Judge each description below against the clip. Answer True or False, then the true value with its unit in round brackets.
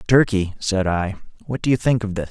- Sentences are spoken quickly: True (235 wpm)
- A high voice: False (105 Hz)